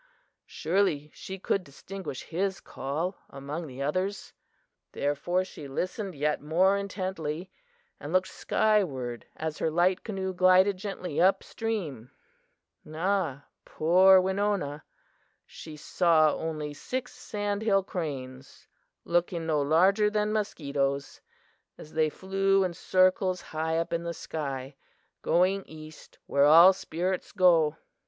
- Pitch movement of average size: Yes, average, 4.2 semitones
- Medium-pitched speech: Yes, medium, 175 Hz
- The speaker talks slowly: Yes, slow, 120 wpm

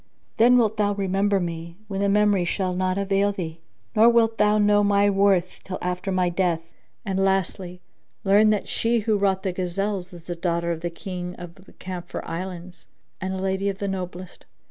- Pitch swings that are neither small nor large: No, narrow, 2.1 semitones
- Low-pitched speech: No, high, 190 Hz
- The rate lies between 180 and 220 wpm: Yes, average, 190 wpm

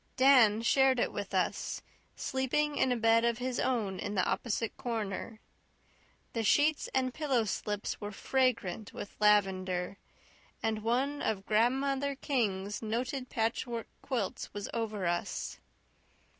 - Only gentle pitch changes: No, average, 3.9 semitones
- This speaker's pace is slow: Yes, slow, 130 wpm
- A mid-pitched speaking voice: No, high, 230 Hz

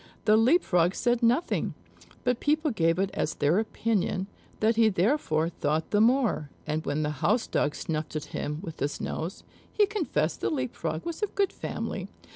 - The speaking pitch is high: Yes, high, 200 Hz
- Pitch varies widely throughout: Yes, wide, 7.7 semitones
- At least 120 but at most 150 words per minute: No, average, 180 wpm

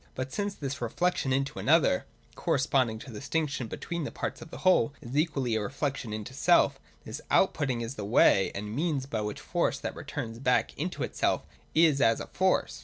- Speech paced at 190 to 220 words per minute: Yes, average, 195 wpm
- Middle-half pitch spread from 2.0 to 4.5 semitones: No, wide, 5.4 semitones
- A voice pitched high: No, low, 135 Hz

